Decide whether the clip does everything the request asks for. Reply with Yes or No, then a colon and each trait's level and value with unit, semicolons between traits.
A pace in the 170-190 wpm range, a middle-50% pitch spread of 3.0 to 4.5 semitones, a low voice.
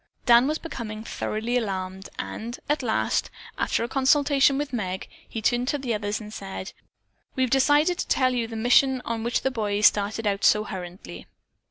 No: average, 185 wpm; average, 4.0 semitones; high, 235 Hz